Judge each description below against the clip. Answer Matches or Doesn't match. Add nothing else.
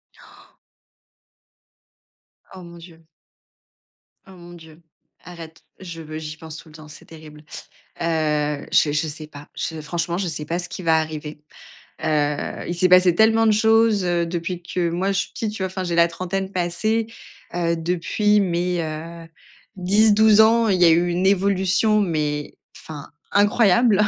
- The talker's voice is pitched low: Doesn't match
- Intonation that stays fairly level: Doesn't match